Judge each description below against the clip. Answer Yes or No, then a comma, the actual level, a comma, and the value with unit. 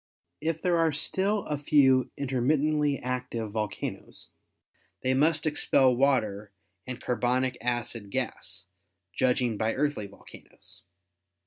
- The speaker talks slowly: Yes, slow, 110 wpm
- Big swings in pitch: No, average, 3.8 semitones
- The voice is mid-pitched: No, low, 130 Hz